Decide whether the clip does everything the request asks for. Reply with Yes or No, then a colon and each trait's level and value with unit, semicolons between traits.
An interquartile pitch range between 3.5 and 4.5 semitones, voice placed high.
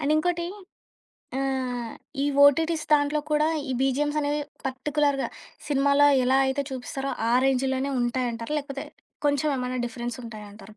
No: narrow, 2.6 semitones; very high, 270 Hz